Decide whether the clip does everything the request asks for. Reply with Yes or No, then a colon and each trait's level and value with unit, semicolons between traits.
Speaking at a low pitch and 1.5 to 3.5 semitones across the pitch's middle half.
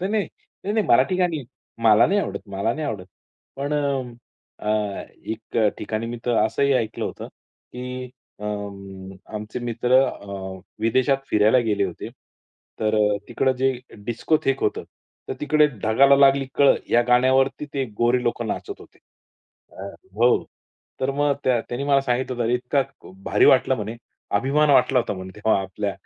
No: low, 125 Hz; average, 4.1 semitones